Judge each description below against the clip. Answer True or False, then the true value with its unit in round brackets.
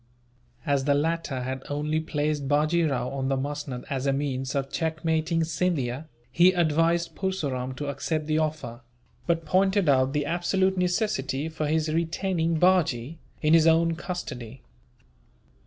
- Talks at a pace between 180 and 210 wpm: False (145 wpm)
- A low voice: False (155 Hz)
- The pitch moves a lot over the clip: False (3.5 semitones)